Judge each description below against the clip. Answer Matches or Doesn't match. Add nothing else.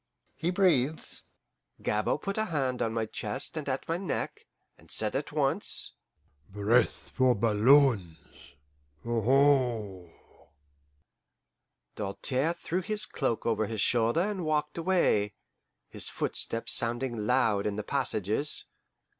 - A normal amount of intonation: Doesn't match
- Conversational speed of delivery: Doesn't match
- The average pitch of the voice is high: Doesn't match